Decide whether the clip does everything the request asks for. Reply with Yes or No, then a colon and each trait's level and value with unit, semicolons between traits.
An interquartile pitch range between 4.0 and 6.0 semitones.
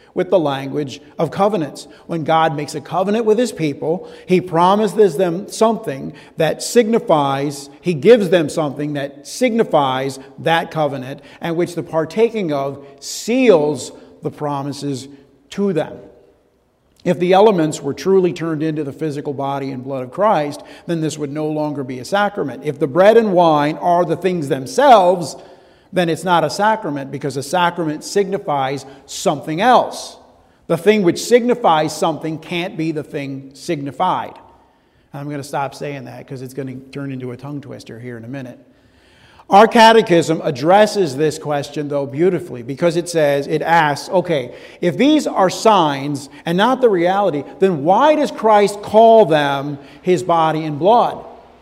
Yes: average, 4.8 semitones